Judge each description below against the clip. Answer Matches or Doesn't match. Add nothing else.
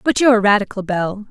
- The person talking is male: Doesn't match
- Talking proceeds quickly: Matches